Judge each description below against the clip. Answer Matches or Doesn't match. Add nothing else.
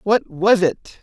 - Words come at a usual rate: Matches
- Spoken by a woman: Doesn't match